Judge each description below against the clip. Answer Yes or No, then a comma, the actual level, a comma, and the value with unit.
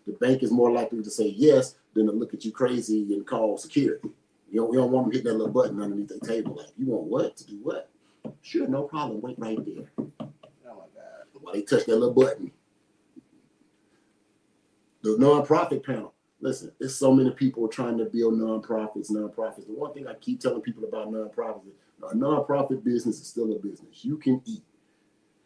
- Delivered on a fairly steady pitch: No, average, 3.3 semitones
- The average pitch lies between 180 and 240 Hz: No, low, 115 Hz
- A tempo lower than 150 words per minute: No, fast, 205 wpm